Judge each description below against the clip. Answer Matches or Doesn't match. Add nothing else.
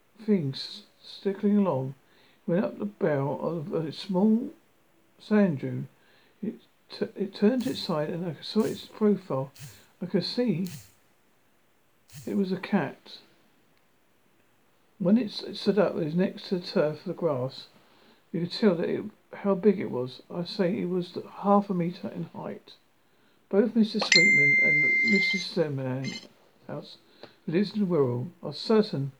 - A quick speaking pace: Doesn't match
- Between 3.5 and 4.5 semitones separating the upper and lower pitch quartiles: Matches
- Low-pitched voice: Doesn't match